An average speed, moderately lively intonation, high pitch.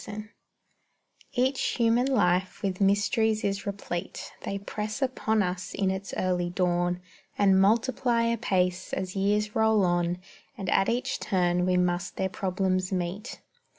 Yes: average, 145 wpm; average, 3.1 semitones; high, 195 Hz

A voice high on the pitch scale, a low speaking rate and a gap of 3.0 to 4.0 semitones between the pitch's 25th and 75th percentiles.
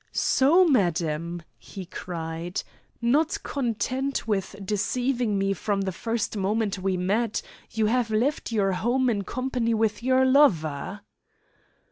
No: high, 215 Hz; slow, 125 wpm; average, 4.8 semitones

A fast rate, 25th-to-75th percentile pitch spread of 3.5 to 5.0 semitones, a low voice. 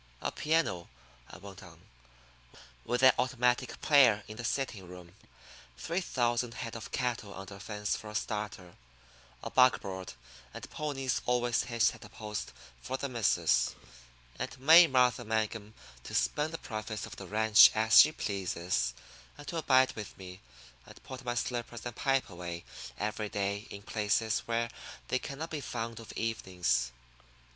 No: average, 155 wpm; average, 4.1 semitones; low, 110 Hz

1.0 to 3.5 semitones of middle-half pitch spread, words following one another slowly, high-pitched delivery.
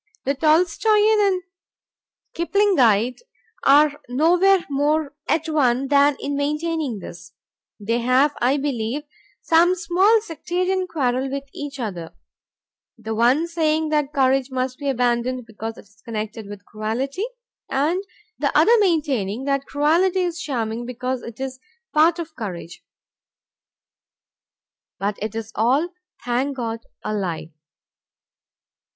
No: wide, 5.6 semitones; slow, 125 wpm; very high, 275 Hz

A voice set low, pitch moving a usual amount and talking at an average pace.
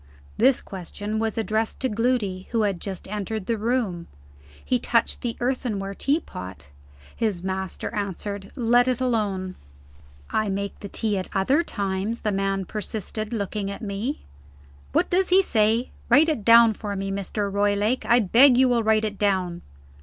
No: high, 210 Hz; average, 3.1 semitones; average, 160 wpm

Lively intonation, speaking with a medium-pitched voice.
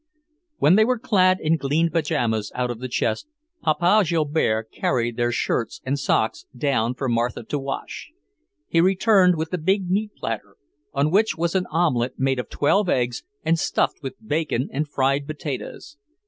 Yes: wide, 6.0 semitones; medium, 150 Hz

